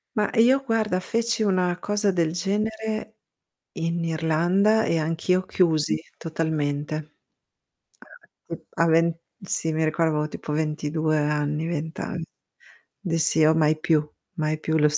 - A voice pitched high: No, medium, 165 Hz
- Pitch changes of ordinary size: Yes, average, 3.3 semitones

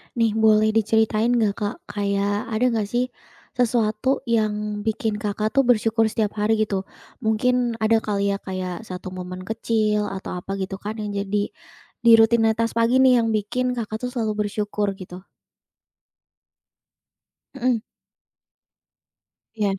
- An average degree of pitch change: No, narrow, 2.0 semitones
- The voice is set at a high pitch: Yes, high, 215 Hz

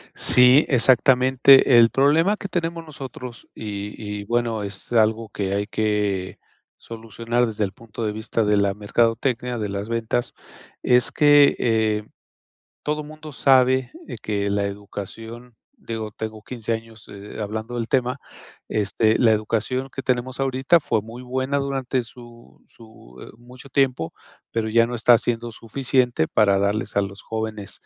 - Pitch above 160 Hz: No, low, 115 Hz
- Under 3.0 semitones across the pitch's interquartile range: No, average, 3.3 semitones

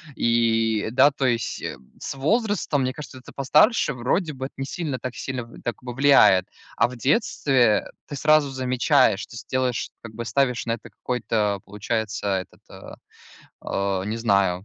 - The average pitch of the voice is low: Yes, low, 125 Hz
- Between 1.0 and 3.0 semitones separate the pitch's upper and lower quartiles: No, average, 3.6 semitones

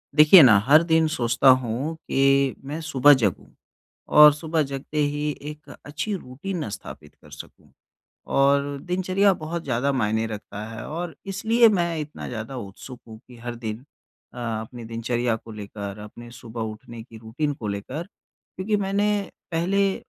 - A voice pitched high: No, low, 135 Hz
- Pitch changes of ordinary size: No, wide, 5.8 semitones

